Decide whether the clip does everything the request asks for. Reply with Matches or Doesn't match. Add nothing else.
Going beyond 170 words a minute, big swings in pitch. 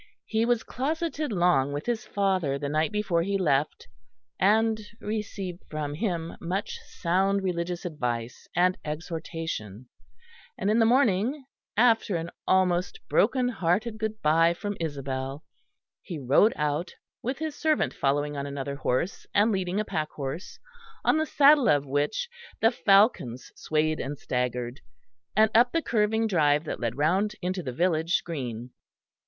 Doesn't match